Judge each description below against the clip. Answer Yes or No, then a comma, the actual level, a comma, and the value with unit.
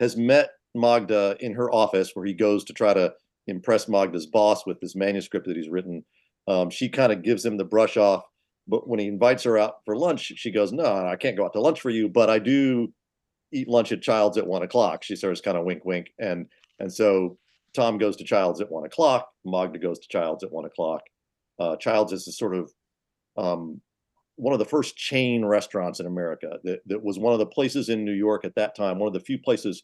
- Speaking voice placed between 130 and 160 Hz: No, low, 105 Hz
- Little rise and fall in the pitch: No, average, 3.7 semitones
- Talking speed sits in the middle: No, fast, 230 wpm